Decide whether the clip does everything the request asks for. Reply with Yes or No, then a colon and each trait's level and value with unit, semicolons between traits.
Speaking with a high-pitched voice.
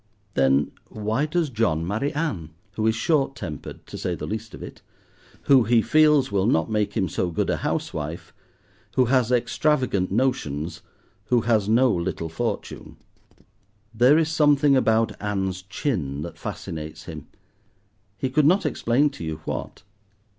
No: low, 110 Hz